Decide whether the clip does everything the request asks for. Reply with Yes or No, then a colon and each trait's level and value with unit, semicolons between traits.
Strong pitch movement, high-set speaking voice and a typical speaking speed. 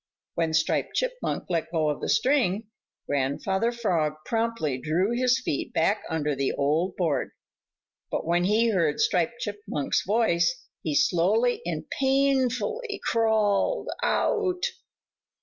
No: wide, 6.8 semitones; high, 195 Hz; slow, 125 wpm